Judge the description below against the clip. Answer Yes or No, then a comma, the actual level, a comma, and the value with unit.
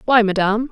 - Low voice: No, high, 220 Hz